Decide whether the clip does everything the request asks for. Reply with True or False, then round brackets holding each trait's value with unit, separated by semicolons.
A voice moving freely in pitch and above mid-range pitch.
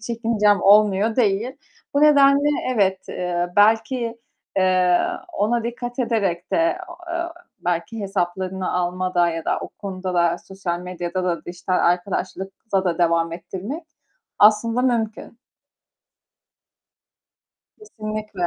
False (4.3 semitones; 195 Hz)